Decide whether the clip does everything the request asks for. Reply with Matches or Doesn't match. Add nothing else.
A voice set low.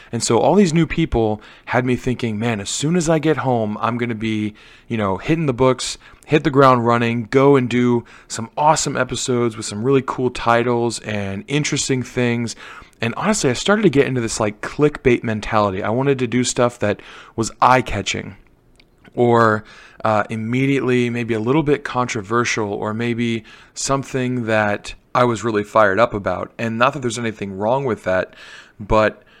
Matches